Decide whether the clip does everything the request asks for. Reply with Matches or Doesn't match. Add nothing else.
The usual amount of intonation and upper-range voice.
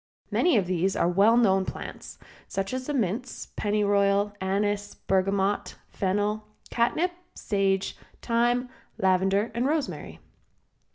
Matches